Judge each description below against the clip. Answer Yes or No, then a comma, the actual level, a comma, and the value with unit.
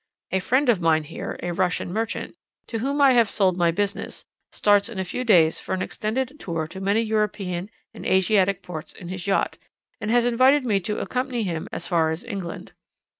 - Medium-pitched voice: No, high, 200 Hz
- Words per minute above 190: Yes, average, 200 wpm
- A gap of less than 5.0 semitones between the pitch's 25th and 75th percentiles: Yes, average, 4.6 semitones